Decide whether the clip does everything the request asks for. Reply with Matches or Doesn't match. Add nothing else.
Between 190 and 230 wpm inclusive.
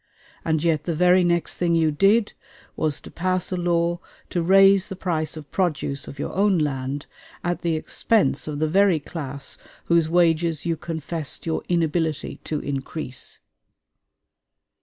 Doesn't match